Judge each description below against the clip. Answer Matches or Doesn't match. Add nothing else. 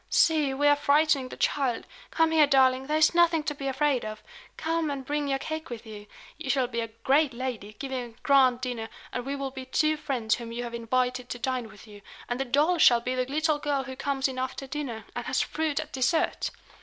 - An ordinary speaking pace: Doesn't match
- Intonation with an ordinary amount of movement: Matches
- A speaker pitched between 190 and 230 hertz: Doesn't match